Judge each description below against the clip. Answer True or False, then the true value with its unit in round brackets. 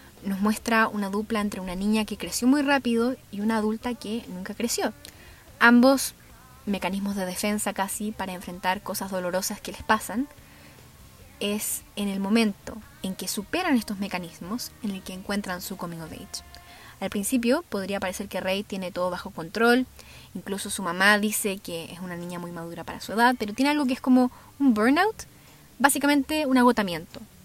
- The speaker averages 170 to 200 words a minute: True (175 wpm)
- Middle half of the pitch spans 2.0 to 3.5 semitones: False (4.0 semitones)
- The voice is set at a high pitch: True (210 Hz)